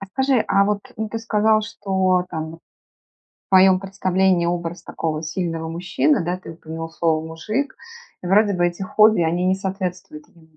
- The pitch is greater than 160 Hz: Yes, medium, 185 Hz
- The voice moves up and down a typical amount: Yes, average, 3.1 semitones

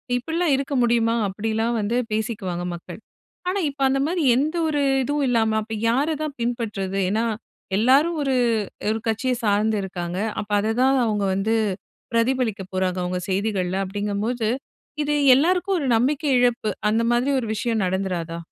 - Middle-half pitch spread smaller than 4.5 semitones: No, average, 4.8 semitones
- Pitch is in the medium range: No, high, 225 Hz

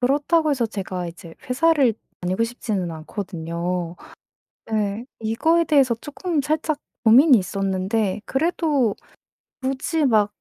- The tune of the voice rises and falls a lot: Yes, wide, 7.2 semitones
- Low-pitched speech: No, high, 225 Hz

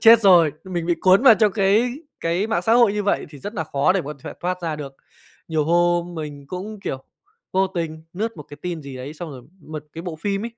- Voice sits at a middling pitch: Yes, medium, 175 Hz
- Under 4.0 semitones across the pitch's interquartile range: No, average, 4.3 semitones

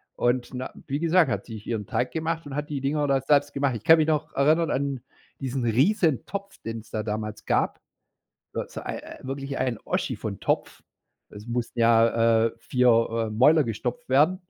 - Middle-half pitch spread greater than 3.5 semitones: Yes, average, 4.6 semitones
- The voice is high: No, low, 135 Hz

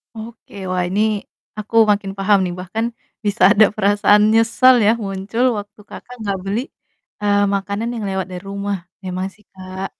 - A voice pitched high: Yes, high, 205 Hz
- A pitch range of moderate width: No, narrow, 2.1 semitones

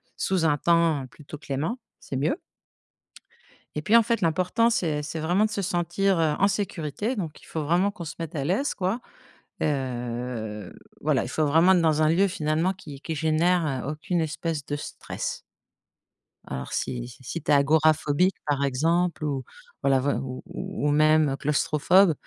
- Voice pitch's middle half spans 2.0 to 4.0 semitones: Yes, average, 3.7 semitones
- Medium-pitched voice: Yes, medium, 155 Hz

